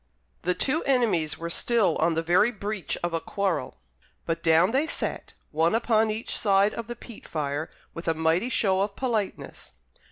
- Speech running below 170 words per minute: No, average, 180 wpm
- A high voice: Yes, high, 195 Hz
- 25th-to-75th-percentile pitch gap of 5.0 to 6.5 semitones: Yes, wide, 5.4 semitones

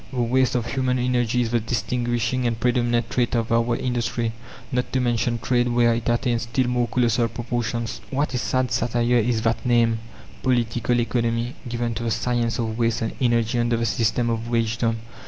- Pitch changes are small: Yes, narrow, 1.0 semitones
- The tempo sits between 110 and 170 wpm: No, average, 185 wpm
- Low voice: Yes, low, 120 Hz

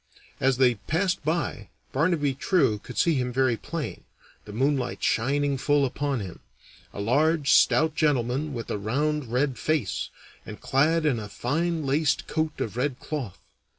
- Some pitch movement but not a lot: Yes, average, 3.8 semitones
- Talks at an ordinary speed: Yes, average, 155 wpm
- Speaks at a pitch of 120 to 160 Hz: Yes, medium, 140 Hz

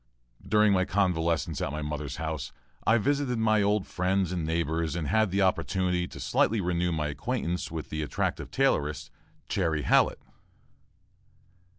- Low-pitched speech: Yes, very low, 90 Hz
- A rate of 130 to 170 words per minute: Yes, average, 150 wpm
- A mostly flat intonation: No, average, 4.4 semitones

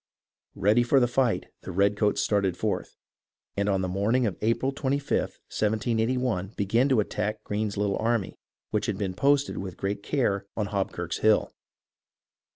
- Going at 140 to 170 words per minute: Yes, average, 160 wpm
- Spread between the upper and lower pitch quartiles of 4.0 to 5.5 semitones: No, average, 3.5 semitones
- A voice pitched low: Yes, low, 105 Hz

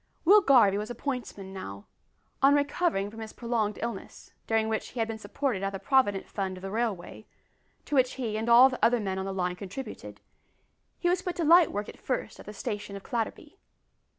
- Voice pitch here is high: Yes, high, 225 Hz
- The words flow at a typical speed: No, fast, 215 wpm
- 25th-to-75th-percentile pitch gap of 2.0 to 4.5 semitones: No, average, 4.9 semitones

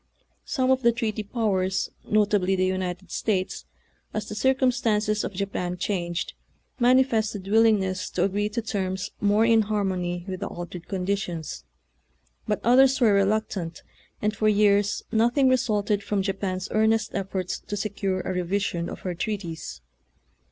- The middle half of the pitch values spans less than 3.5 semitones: Yes, average, 2.7 semitones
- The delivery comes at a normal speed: Yes, average, 150 wpm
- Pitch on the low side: No, high, 205 Hz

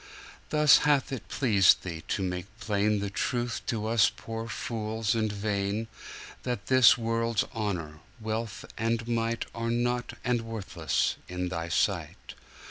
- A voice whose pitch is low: Yes, low, 110 Hz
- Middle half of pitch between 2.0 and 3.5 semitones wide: Yes, average, 2.7 semitones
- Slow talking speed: Yes, slow, 130 wpm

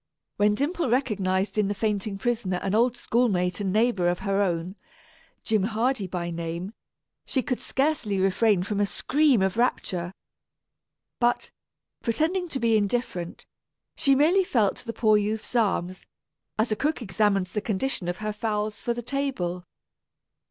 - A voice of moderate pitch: No, high, 215 Hz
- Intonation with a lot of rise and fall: No, average, 4.2 semitones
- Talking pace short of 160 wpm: Yes, average, 150 wpm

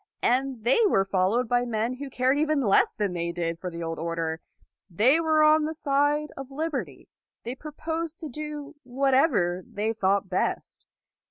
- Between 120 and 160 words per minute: No, average, 170 wpm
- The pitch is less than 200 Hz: No, very high, 250 Hz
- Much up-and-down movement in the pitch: Yes, wide, 7.6 semitones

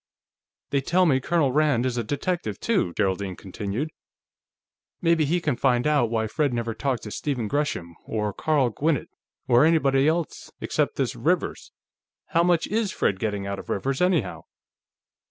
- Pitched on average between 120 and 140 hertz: Yes, low, 135 Hz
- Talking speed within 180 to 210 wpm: No, average, 160 wpm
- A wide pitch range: Yes, wide, 6.1 semitones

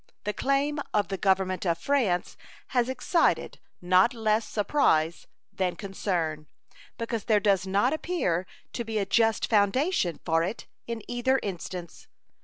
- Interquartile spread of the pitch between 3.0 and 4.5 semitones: No, average, 4.9 semitones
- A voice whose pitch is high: Yes, high, 205 Hz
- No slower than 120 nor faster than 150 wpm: Yes, average, 140 wpm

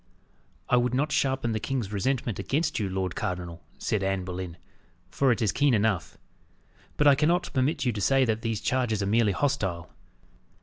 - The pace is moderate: Yes, average, 180 wpm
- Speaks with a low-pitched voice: Yes, low, 115 Hz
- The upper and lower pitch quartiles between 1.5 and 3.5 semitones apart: No, wide, 5.6 semitones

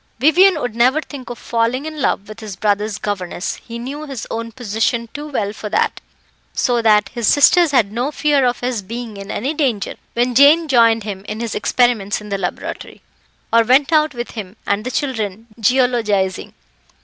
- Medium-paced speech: Yes, average, 185 wpm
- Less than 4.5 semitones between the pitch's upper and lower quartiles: Yes, average, 4.1 semitones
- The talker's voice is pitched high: Yes, high, 235 Hz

